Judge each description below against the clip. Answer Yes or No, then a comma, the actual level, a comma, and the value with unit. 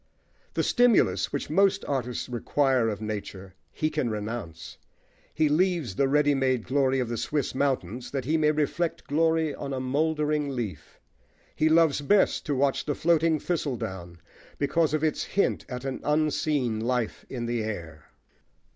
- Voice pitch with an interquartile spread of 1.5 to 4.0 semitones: No, average, 4.6 semitones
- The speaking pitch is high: No, medium, 140 Hz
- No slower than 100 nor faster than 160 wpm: Yes, average, 155 wpm